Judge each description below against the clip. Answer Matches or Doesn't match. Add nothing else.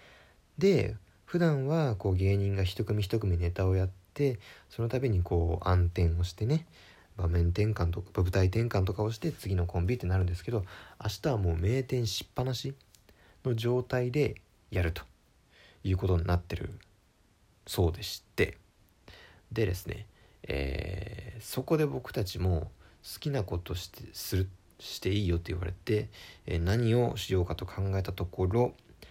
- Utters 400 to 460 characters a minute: Doesn't match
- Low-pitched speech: Matches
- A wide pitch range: Doesn't match